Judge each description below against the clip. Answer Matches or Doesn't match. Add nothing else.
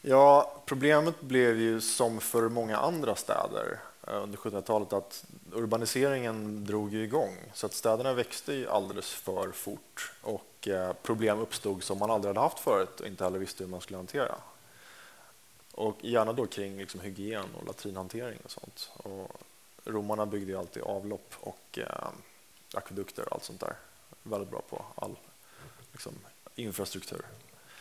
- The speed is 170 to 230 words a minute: Doesn't match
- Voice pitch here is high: Doesn't match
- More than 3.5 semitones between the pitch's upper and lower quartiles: Doesn't match